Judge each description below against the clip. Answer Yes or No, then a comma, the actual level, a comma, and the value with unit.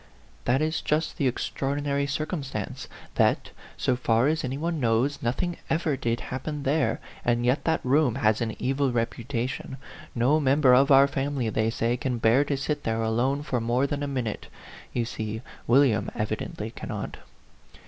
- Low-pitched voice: Yes, low, 130 Hz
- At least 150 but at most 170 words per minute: Yes, average, 165 wpm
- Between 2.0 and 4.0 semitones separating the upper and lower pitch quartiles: Yes, average, 3.3 semitones